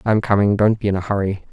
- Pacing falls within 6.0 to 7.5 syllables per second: Yes, 6.6 syllables/s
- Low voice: Yes, low, 100 Hz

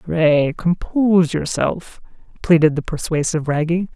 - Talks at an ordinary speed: No, slow, 105 wpm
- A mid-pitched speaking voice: Yes, medium, 165 Hz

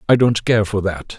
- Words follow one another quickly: Yes, fast, 255 wpm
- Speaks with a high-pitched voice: No, low, 105 Hz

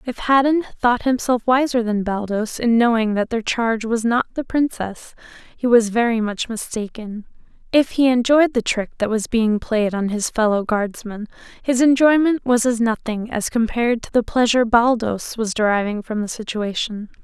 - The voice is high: Yes, high, 230 Hz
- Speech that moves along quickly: No, average, 175 wpm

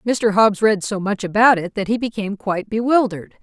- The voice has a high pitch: Yes, high, 210 Hz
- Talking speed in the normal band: No, fast, 210 wpm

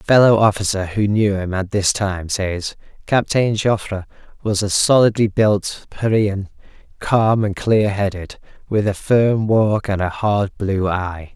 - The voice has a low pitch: Yes, low, 100 Hz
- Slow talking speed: No, average, 160 wpm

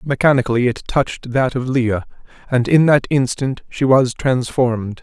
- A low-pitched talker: Yes, low, 130 Hz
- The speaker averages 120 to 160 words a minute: Yes, average, 155 wpm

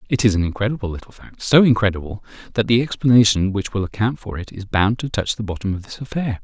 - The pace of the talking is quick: Yes, fast, 235 wpm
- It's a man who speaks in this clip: Yes, male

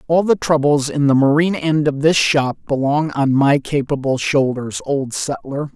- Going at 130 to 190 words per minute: Yes, average, 175 wpm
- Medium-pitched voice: Yes, medium, 145 Hz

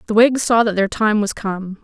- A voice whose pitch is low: No, high, 215 Hz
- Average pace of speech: No, fast, 260 wpm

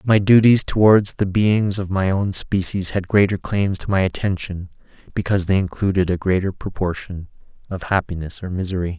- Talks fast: No, average, 165 wpm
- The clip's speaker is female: No, male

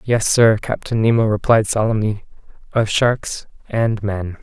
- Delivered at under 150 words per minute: Yes, slow, 135 wpm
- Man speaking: Yes, male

